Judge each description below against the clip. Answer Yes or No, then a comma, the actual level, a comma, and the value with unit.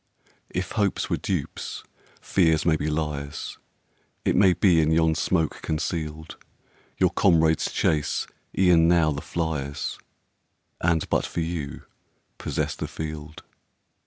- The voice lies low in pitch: Yes, very low, 80 Hz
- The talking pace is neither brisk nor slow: No, slow, 110 wpm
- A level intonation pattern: Yes, narrow, 1.8 semitones